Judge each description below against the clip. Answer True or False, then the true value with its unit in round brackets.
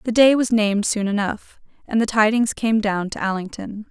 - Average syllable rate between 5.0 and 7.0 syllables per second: True (5.1 syllables/s)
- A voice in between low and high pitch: False (215 Hz)